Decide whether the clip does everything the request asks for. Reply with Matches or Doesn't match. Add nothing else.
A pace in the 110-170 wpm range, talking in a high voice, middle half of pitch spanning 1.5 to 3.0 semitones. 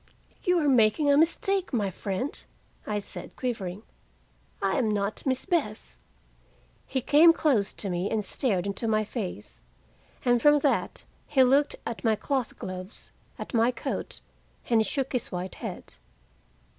Doesn't match